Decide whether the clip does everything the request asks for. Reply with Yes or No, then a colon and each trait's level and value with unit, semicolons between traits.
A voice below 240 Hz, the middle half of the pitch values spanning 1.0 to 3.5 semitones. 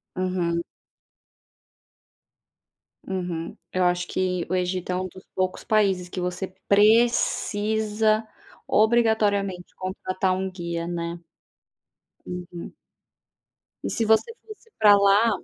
Yes: medium, 185 Hz; average, 3.1 semitones